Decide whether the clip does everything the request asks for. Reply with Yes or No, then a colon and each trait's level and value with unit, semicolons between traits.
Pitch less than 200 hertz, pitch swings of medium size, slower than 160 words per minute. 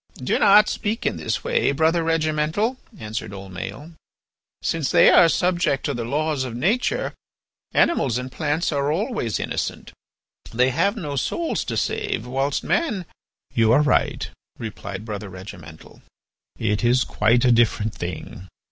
No: medium, 140 Hz; wide, 7.1 semitones; average, 145 wpm